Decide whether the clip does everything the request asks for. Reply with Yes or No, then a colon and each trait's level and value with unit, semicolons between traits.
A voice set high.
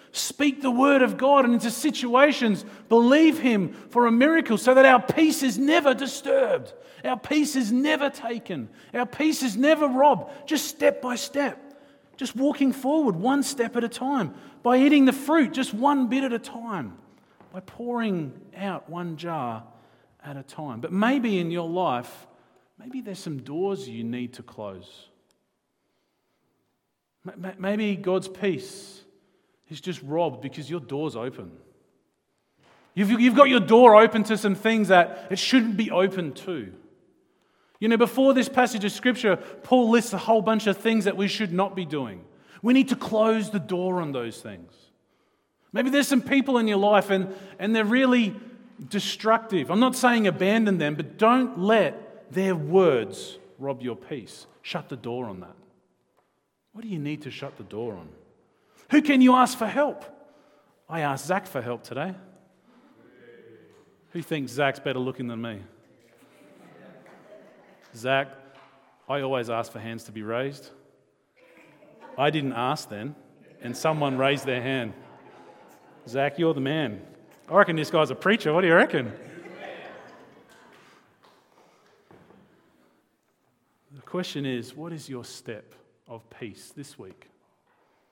Yes: high, 200 Hz